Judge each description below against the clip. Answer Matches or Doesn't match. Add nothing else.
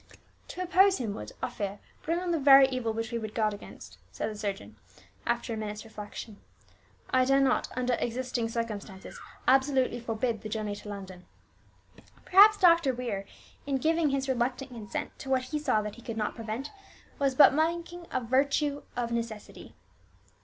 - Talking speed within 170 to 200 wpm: Matches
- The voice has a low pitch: Doesn't match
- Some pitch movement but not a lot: Matches